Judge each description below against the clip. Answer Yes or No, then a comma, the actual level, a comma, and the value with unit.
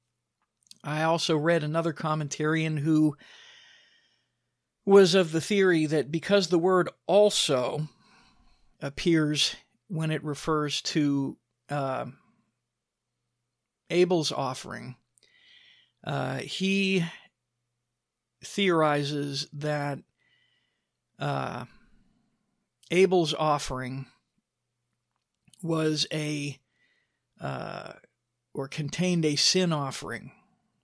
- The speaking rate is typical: No, slow, 75 wpm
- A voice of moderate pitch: Yes, medium, 155 Hz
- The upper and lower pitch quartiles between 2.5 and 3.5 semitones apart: No, average, 4.3 semitones